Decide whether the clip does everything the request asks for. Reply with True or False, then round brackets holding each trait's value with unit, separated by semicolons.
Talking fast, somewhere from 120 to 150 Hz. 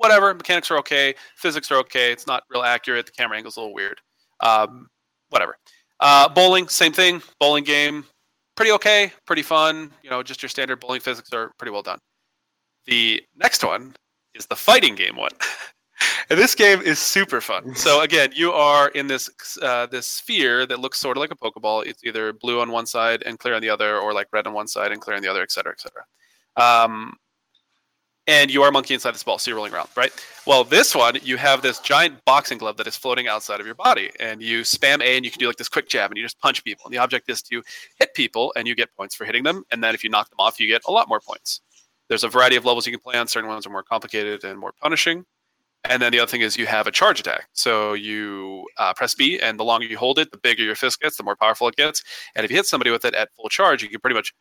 True (260 wpm; 125 Hz)